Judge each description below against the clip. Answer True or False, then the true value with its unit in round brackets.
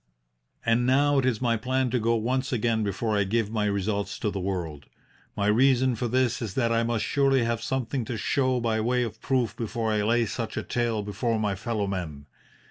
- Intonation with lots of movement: False (3.1 semitones)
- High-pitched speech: False (115 Hz)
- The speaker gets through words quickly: True (215 wpm)